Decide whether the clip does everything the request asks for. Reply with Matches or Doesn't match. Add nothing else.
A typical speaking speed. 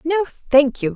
Matches